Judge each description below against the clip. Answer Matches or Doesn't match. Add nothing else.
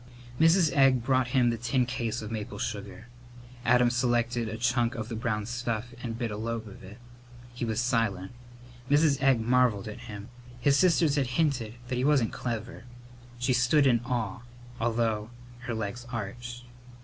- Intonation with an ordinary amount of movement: Doesn't match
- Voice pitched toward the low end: Matches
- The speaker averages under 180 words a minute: Matches